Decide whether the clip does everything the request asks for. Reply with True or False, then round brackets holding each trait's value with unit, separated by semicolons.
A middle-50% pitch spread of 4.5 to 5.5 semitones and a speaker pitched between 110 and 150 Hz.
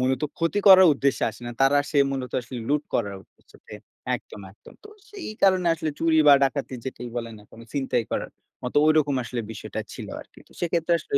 True (4.9 semitones; 140 Hz)